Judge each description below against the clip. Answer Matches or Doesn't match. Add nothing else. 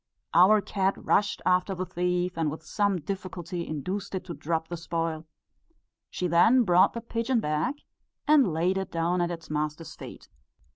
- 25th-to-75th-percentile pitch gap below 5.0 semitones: Matches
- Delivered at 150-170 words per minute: Matches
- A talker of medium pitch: Matches